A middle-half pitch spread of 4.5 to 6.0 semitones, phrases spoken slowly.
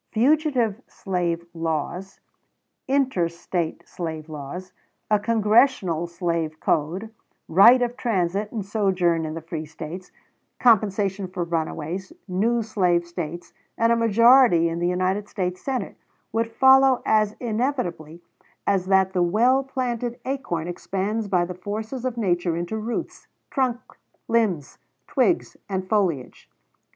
Yes: average, 5.1 semitones; slow, 125 wpm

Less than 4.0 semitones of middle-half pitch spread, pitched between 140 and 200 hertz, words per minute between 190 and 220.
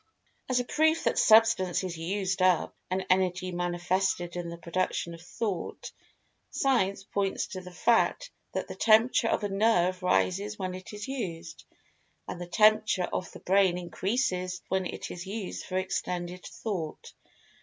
No: average, 2.9 semitones; medium, 185 Hz; average, 155 wpm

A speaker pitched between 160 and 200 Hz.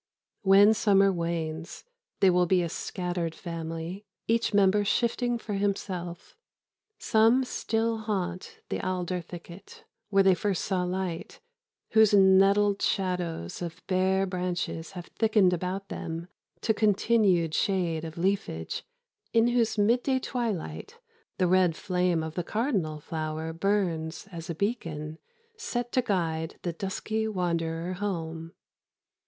Yes: medium, 185 Hz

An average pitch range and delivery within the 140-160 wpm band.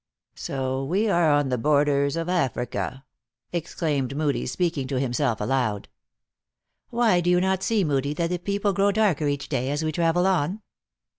No: average, 4.7 semitones; average, 170 wpm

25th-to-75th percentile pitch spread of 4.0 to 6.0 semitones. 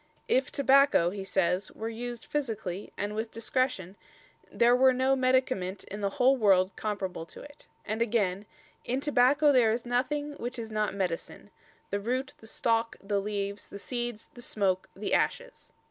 Yes: average, 4.3 semitones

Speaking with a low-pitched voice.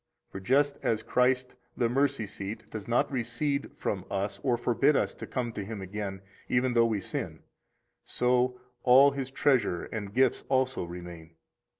Yes: low, 120 Hz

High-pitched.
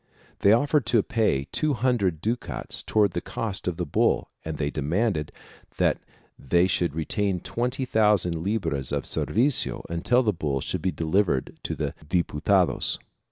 No: very low, 95 Hz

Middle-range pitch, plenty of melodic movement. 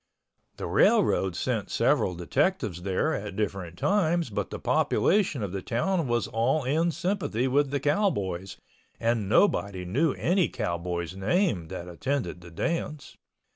No: low, 120 Hz; wide, 9.0 semitones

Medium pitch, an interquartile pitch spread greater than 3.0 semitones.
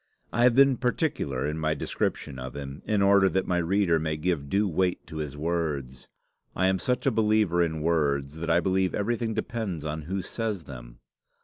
No: very low, 85 Hz; average, 5.2 semitones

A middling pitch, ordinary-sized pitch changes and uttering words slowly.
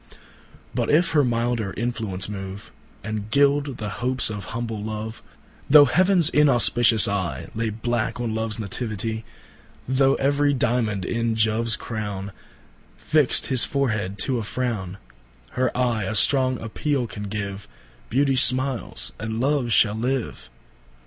No: low, 115 Hz; average, 3.8 semitones; slow, 115 wpm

